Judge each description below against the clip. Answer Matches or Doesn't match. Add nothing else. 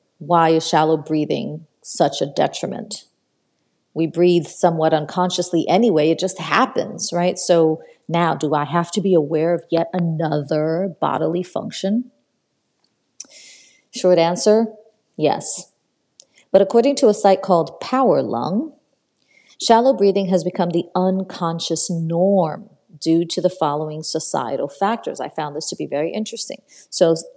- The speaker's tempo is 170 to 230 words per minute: Doesn't match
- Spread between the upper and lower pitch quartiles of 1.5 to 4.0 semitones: Doesn't match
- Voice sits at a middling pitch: Matches